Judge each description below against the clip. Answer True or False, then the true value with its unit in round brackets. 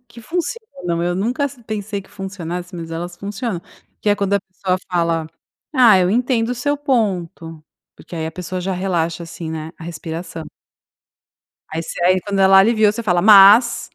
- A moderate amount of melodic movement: True (4.2 semitones)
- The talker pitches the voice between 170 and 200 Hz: True (190 Hz)